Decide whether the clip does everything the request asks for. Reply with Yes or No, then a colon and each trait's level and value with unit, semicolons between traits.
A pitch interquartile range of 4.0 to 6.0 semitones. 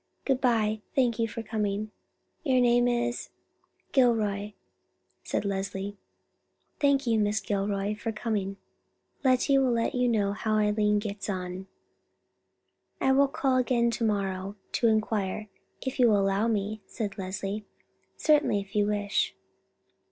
No: average, 3.1 semitones